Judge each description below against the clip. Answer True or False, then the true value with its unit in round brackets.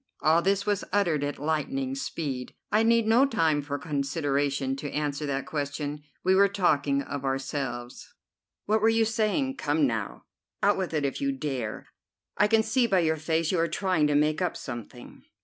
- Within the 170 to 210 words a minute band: True (185 wpm)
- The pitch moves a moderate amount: False (6.1 semitones)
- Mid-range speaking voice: True (155 Hz)